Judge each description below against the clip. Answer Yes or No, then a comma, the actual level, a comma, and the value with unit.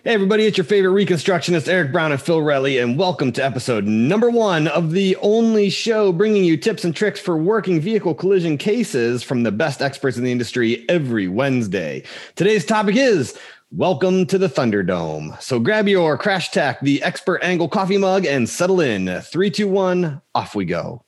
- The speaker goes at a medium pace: Yes, average, 180 wpm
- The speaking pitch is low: No, medium, 175 Hz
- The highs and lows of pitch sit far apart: Yes, wide, 6.2 semitones